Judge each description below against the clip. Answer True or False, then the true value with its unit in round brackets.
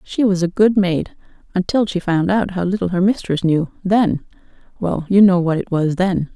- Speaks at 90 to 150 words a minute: False (190 wpm)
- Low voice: False (185 Hz)